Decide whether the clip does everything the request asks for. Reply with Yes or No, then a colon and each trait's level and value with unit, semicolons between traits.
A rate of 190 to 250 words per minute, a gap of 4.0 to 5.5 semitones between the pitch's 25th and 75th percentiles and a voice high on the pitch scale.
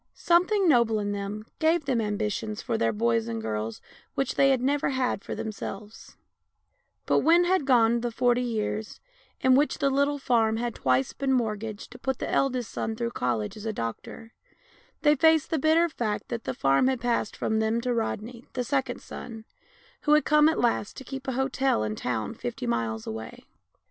Yes: average, 195 wpm; average, 4.5 semitones; high, 235 Hz